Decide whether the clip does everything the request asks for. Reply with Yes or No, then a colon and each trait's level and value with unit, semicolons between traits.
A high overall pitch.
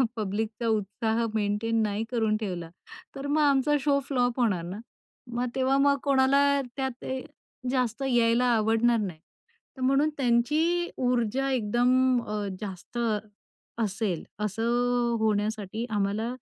Yes: high, 235 Hz